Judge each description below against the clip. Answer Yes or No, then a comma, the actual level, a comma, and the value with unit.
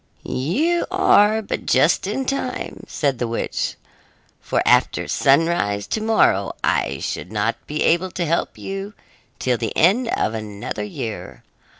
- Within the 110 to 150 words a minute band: Yes, average, 140 wpm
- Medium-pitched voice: Yes, medium, 165 Hz